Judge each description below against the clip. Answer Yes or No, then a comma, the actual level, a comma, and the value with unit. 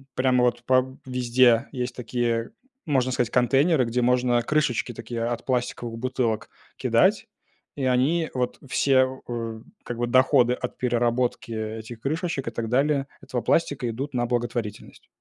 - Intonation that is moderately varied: No, narrow, 1.7 semitones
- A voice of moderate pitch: No, low, 125 Hz